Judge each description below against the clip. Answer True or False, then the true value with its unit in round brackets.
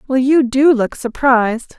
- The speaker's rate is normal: True (170 wpm)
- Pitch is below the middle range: False (255 Hz)